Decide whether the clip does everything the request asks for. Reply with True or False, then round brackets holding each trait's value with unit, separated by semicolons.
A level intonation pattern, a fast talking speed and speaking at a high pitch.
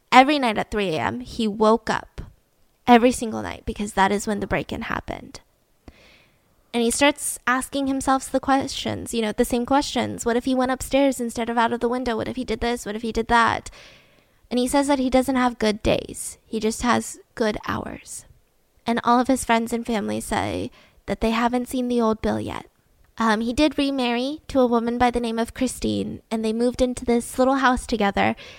True (2.2 semitones; 210 wpm; 240 Hz)